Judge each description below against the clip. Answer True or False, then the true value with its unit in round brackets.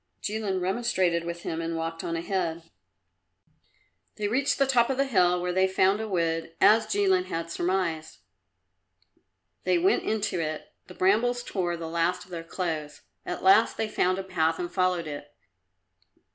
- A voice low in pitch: False (180 Hz)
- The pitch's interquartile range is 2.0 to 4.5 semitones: True (3.6 semitones)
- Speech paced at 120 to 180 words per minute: True (165 wpm)